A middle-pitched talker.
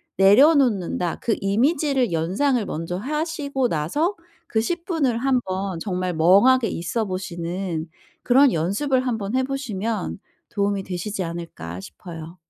No: high, 205 Hz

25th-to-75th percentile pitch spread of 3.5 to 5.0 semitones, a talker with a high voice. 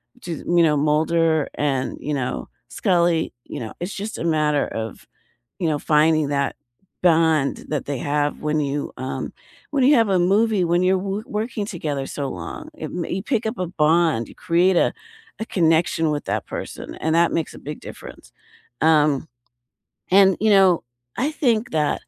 No: average, 4.2 semitones; medium, 165 Hz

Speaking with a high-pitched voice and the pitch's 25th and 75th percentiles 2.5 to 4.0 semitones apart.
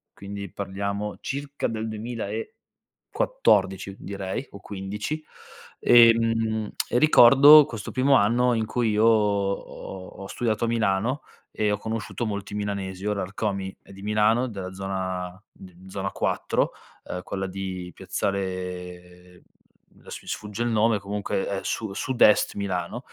No: low, 100 Hz; average, 2.8 semitones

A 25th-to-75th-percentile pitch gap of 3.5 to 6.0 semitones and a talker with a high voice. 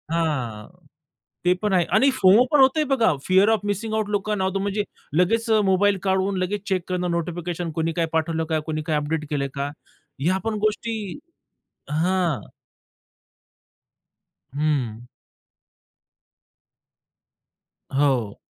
No: average, 4.5 semitones; medium, 180 Hz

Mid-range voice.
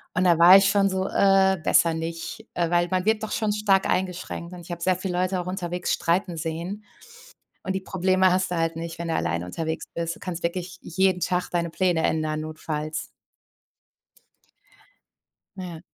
Yes: medium, 180 Hz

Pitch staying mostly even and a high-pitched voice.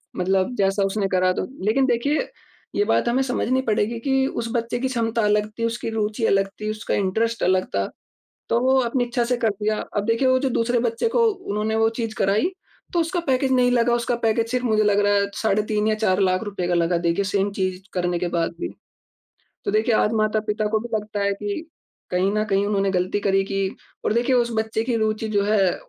No: average, 3.2 semitones; high, 215 Hz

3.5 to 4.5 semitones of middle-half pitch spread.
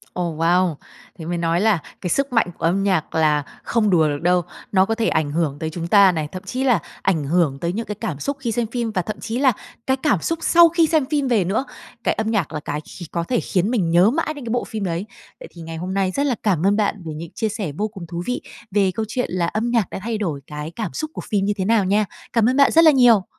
No: wide, 5.5 semitones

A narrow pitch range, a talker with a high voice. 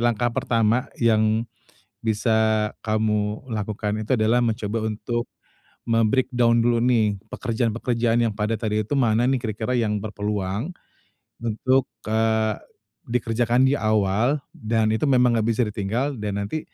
No: narrow, 2.0 semitones; low, 115 Hz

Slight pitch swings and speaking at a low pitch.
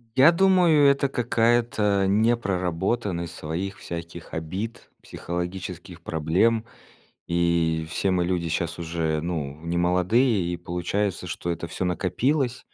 No: average, 5.0 semitones; very low, 90 Hz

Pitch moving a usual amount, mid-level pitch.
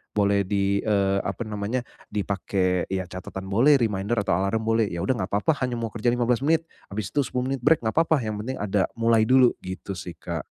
No: average, 3.8 semitones; low, 105 Hz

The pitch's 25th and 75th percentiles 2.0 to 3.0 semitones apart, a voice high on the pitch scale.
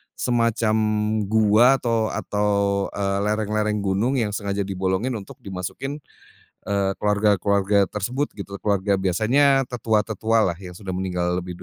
No: narrow, 2.4 semitones; low, 105 Hz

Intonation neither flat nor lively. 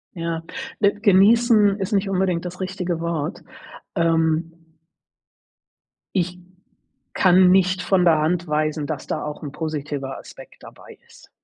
Yes: average, 3.1 semitones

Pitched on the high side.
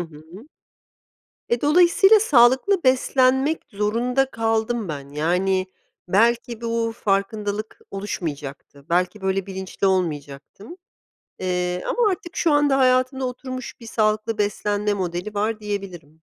Yes: high, 215 Hz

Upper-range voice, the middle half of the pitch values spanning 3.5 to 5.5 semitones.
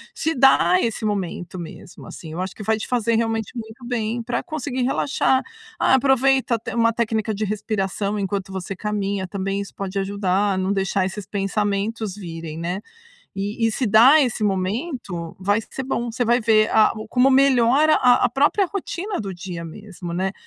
Yes: high, 215 Hz; average, 4.0 semitones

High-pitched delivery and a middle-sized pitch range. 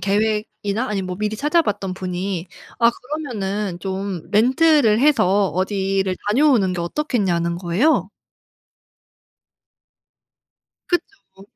Yes: high, 205 Hz; average, 4.7 semitones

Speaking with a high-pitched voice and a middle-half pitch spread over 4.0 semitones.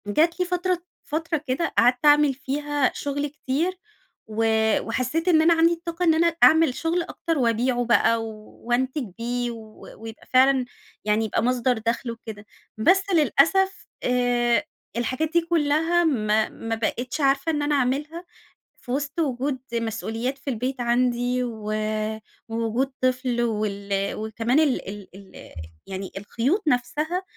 Yes: very high, 255 Hz; average, 5.0 semitones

